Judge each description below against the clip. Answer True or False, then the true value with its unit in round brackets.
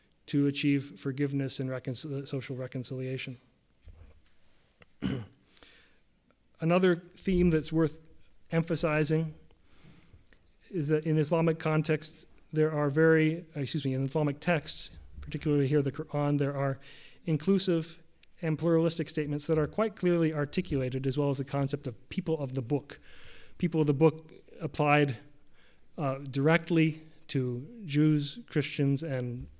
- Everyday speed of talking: False (120 wpm)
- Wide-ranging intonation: False (3.0 semitones)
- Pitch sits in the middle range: True (150 Hz)